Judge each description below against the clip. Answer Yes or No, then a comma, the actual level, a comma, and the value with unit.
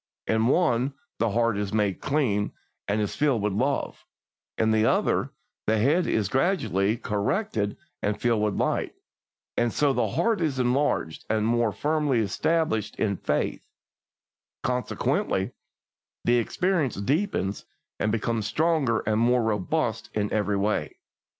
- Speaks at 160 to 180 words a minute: No, slow, 135 wpm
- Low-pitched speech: Yes, low, 115 Hz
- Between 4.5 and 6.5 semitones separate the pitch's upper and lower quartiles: Yes, average, 4.8 semitones